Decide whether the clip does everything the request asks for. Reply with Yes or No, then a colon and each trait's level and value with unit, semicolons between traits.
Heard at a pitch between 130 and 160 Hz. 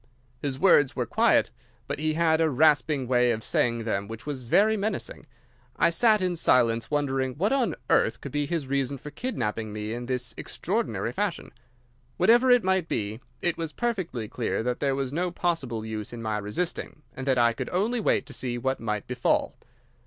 Yes: low, 135 Hz